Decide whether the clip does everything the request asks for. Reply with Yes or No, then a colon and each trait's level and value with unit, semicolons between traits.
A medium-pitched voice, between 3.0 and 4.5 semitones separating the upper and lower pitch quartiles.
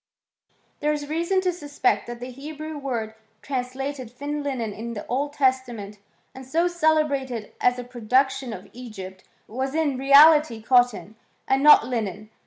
No: very high, 260 Hz; average, 3.5 semitones